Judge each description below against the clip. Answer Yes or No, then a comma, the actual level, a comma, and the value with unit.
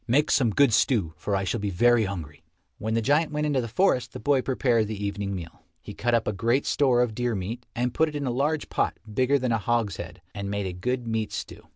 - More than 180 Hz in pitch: No, low, 115 Hz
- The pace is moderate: No, fast, 250 wpm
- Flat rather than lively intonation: No, average, 4.2 semitones